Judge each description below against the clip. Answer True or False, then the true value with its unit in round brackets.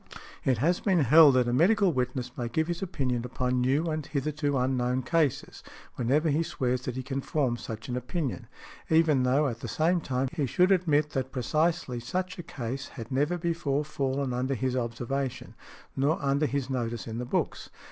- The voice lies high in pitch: False (135 Hz)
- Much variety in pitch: False (3.8 semitones)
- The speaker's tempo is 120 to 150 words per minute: False (190 wpm)